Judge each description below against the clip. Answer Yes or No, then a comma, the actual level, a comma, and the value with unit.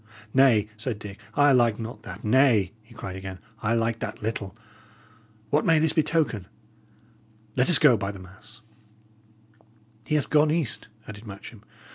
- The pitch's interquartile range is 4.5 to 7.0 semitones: Yes, average, 4.8 semitones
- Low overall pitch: Yes, low, 115 Hz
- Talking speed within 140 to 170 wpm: Yes, average, 155 wpm